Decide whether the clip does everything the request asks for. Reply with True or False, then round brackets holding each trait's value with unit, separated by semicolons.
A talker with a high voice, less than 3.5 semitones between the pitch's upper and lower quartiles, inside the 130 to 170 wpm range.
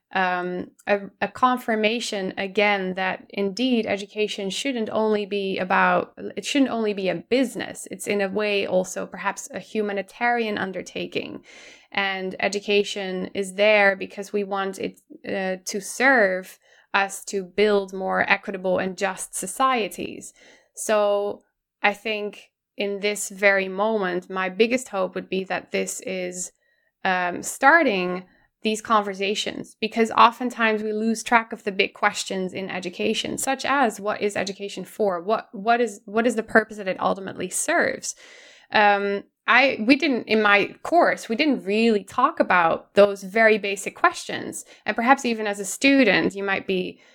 True (205 Hz; 2.6 semitones; 150 wpm)